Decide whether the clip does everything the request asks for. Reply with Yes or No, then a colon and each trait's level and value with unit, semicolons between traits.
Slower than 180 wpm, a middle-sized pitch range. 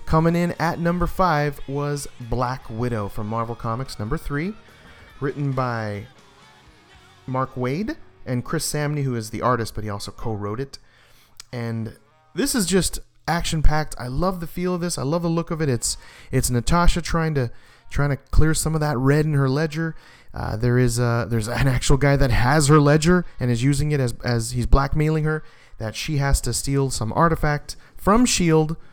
No: average, 190 wpm; average, 4.8 semitones